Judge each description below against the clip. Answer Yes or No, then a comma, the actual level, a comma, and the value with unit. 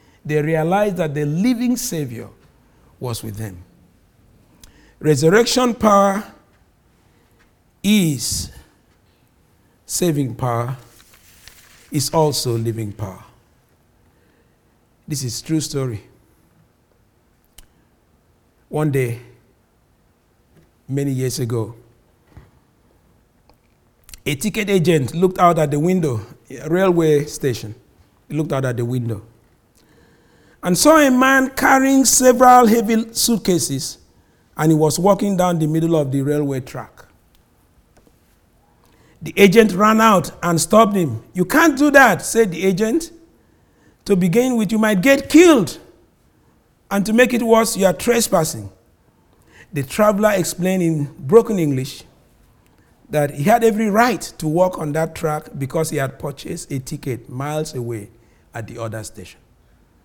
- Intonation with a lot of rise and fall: Yes, wide, 8.7 semitones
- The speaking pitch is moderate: Yes, medium, 155 Hz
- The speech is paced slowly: Yes, slow, 120 wpm